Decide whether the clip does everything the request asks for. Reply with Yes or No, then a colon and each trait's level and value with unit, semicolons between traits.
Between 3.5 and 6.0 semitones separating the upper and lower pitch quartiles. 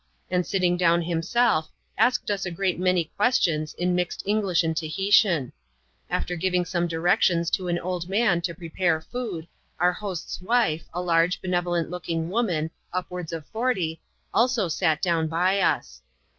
No: narrow, 2.6 semitones